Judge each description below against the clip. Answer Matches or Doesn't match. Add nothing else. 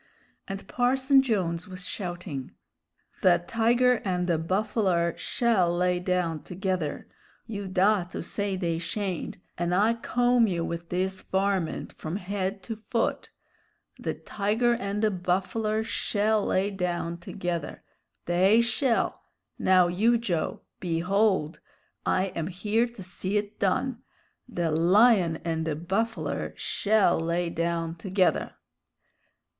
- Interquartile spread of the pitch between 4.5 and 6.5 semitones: Doesn't match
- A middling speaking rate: Doesn't match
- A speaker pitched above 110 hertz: Matches